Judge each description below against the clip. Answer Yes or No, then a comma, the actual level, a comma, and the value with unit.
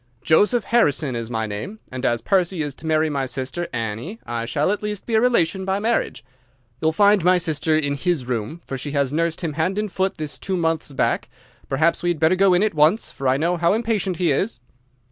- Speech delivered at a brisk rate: Yes, fast, 225 wpm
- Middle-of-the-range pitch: Yes, medium, 160 Hz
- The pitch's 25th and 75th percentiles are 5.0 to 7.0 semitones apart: Yes, wide, 5.4 semitones